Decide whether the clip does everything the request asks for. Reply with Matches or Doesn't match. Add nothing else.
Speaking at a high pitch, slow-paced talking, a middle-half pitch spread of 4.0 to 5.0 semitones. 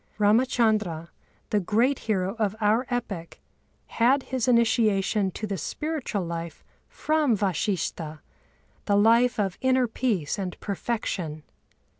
Matches